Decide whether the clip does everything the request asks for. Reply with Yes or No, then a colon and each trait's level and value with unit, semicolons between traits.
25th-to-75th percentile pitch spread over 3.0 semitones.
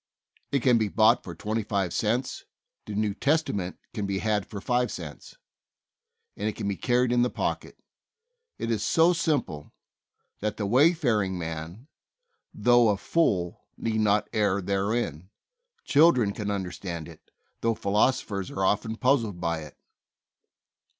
Yes: average, 3.8 semitones